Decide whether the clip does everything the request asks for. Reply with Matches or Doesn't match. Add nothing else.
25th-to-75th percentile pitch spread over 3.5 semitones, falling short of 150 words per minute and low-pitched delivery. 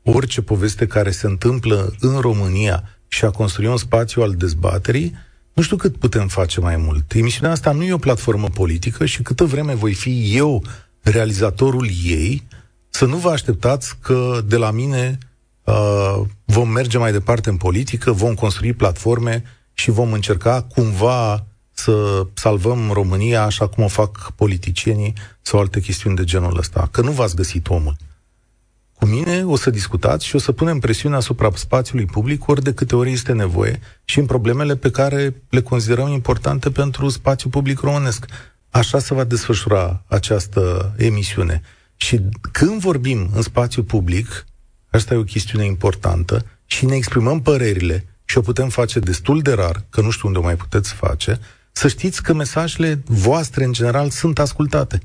Doesn't match